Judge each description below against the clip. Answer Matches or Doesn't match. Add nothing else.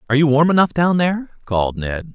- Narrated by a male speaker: Matches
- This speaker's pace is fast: Matches